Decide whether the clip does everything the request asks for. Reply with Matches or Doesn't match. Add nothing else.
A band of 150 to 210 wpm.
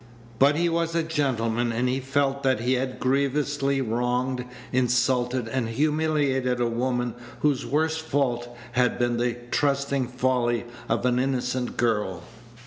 Doesn't match